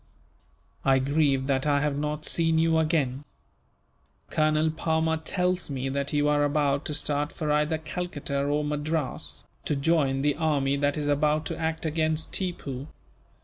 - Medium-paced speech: Yes, average, 155 wpm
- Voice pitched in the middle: Yes, medium, 150 Hz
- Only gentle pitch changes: Yes, narrow, 2.0 semitones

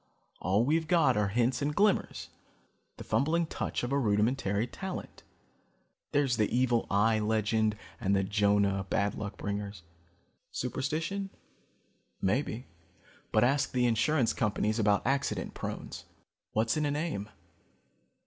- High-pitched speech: No, low, 115 Hz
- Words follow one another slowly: Yes, slow, 130 wpm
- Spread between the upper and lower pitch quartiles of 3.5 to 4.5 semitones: No, wide, 5.4 semitones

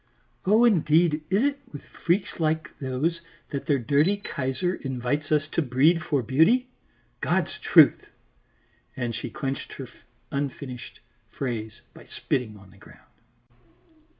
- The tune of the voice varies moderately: Yes, average, 4.5 semitones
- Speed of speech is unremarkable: No, slow, 130 wpm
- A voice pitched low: No, medium, 145 Hz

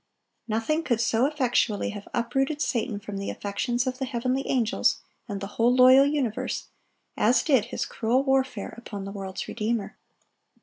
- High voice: Yes, high, 235 Hz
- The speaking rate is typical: Yes, average, 160 wpm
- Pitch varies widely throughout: No, average, 3.8 semitones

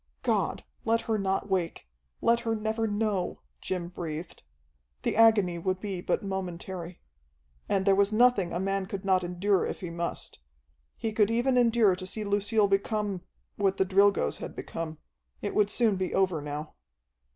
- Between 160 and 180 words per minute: Yes, average, 165 wpm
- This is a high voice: Yes, high, 195 Hz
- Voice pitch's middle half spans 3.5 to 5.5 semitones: No, average, 2.9 semitones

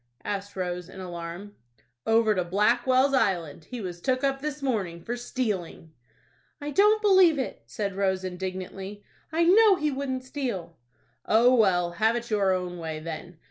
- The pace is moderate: Yes, average, 160 wpm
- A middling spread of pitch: No, wide, 6.5 semitones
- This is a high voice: Yes, high, 205 Hz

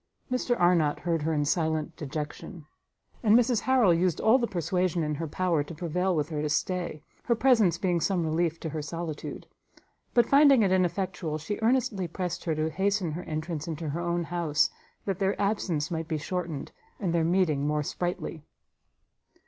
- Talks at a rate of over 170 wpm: Yes, average, 180 wpm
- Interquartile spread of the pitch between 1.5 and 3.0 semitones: No, average, 3.4 semitones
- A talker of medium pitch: Yes, medium, 170 Hz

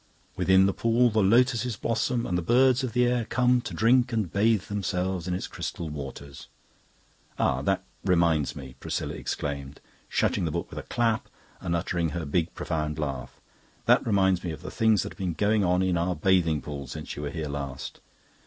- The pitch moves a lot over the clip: Yes, wide, 6.4 semitones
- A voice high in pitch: No, very low, 90 Hz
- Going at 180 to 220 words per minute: Yes, average, 200 wpm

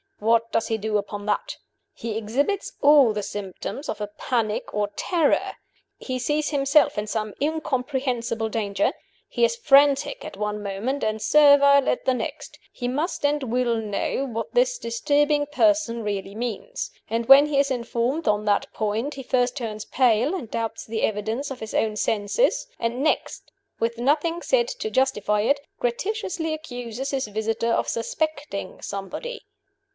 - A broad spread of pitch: No, average, 5.0 semitones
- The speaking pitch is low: No, high, 245 Hz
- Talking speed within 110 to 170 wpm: Yes, average, 160 wpm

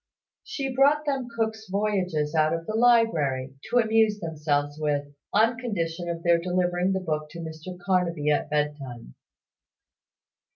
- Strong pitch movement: Yes, wide, 6.3 semitones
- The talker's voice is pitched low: No, medium, 175 Hz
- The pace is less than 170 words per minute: Yes, average, 140 wpm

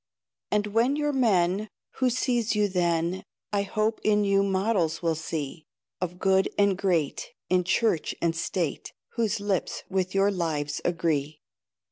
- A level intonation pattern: No, average, 3.7 semitones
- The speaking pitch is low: No, high, 190 Hz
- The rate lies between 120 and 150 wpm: Yes, average, 145 wpm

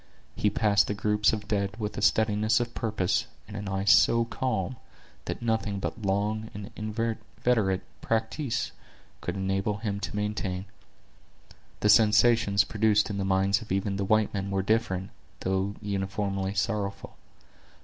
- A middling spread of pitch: No, narrow, 1.9 semitones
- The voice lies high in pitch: No, low, 105 Hz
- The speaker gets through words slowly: No, average, 150 wpm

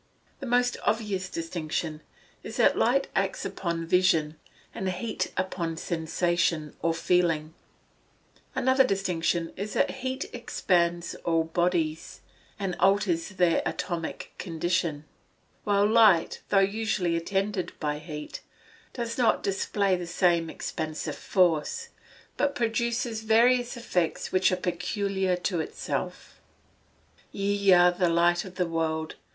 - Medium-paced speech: No, slow, 125 wpm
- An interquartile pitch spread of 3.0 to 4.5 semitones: Yes, average, 3.5 semitones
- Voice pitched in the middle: Yes, medium, 180 Hz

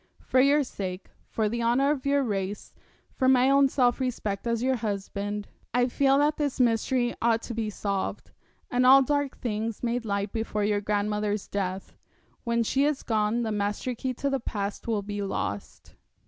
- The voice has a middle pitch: No, high, 230 Hz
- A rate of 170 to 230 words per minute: Yes, average, 180 wpm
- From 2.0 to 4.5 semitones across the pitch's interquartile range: Yes, average, 4.1 semitones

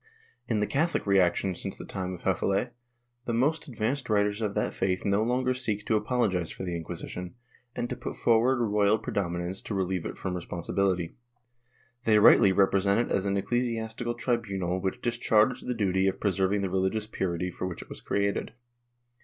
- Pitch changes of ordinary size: Yes, average, 3.6 semitones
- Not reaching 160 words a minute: No, average, 185 wpm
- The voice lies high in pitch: No, low, 100 Hz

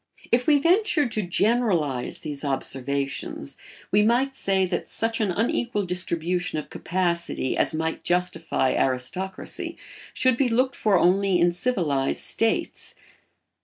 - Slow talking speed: Yes, slow, 130 wpm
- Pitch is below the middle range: No, medium, 185 Hz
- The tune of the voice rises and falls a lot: Yes, wide, 5.9 semitones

